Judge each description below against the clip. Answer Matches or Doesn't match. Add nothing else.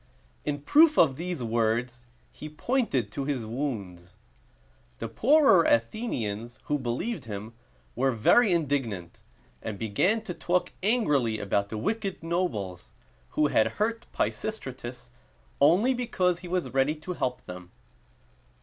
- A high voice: Doesn't match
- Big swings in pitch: Matches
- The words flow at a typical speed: Doesn't match